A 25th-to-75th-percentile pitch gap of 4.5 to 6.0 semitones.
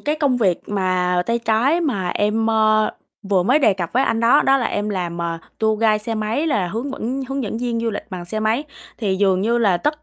No: average, 3.9 semitones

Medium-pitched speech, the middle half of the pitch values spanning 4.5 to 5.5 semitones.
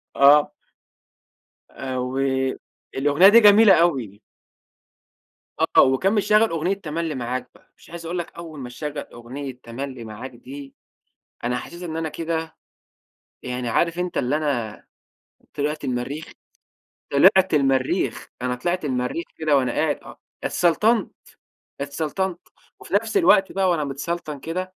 Yes: medium, 150 Hz; average, 4.9 semitones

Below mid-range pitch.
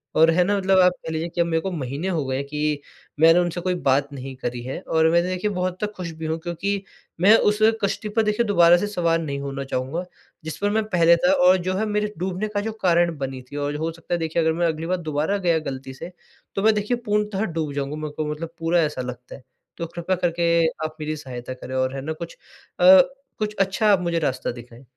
No: medium, 165 Hz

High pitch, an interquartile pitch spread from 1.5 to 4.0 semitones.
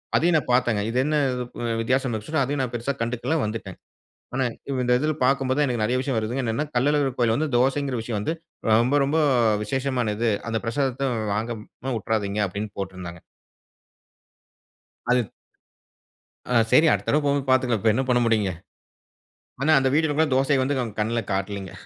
No: low, 125 Hz; average, 3.7 semitones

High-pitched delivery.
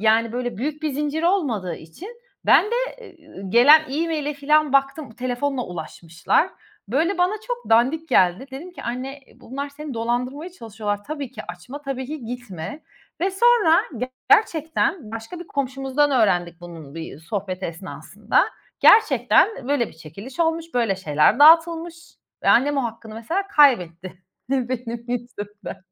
Yes: very high, 260 Hz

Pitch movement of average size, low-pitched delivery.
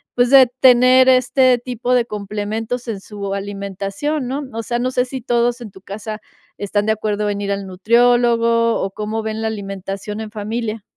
No: average, 3.1 semitones; high, 220 Hz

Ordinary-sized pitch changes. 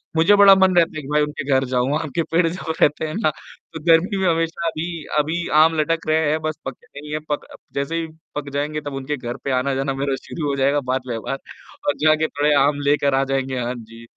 Yes: average, 3.1 semitones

